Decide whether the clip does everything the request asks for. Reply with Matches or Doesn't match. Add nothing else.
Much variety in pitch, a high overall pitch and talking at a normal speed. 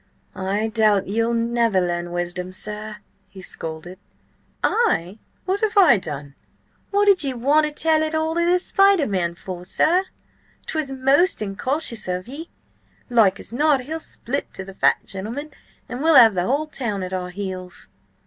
Matches